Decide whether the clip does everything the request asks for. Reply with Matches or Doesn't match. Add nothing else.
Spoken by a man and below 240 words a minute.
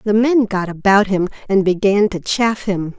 Doesn't match